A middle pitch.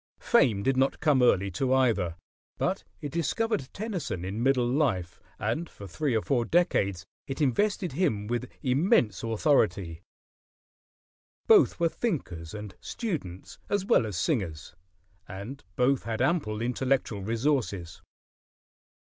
No: low, 125 Hz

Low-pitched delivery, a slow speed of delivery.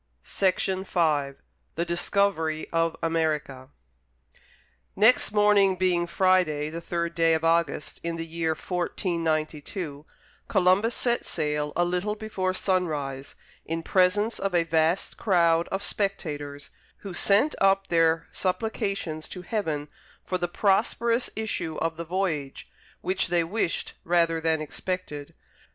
No: medium, 170 Hz; slow, 125 wpm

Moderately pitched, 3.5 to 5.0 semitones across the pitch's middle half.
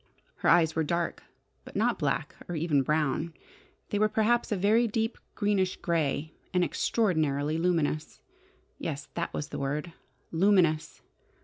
Yes: medium, 170 Hz; average, 4.7 semitones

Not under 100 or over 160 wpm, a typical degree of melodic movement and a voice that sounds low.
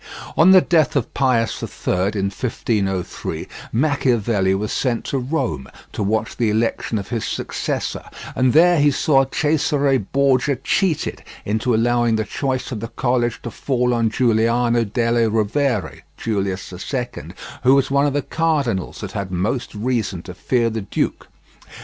Yes: average, 155 wpm; average, 4.0 semitones; low, 120 Hz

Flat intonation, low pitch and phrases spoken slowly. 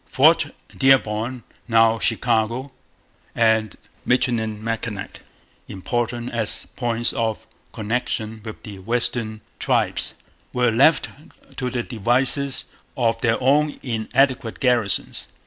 Yes: narrow, 2.1 semitones; low, 115 Hz; slow, 95 wpm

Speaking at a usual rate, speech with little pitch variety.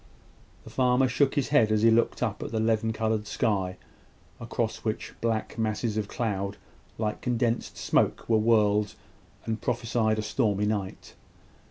Yes: average, 155 wpm; narrow, 1.6 semitones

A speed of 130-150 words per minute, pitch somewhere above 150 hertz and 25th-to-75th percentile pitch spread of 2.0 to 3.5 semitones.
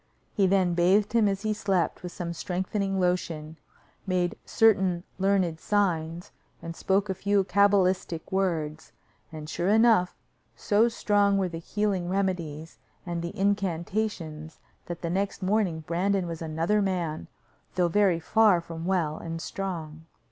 Yes: average, 140 wpm; medium, 185 Hz; average, 3.1 semitones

